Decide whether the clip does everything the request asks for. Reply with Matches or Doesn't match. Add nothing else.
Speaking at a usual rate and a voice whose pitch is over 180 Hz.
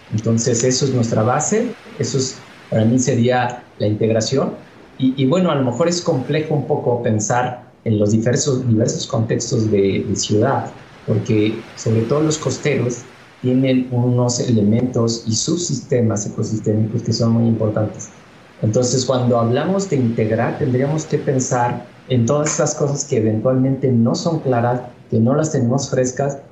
Doesn't match